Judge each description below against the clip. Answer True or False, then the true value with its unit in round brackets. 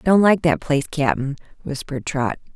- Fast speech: False (165 wpm)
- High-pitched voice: False (150 Hz)